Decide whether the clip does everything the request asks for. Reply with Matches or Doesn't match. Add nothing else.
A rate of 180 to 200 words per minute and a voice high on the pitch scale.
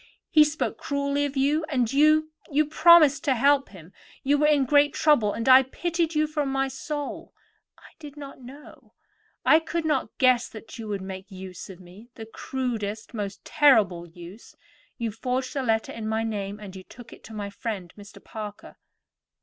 Matches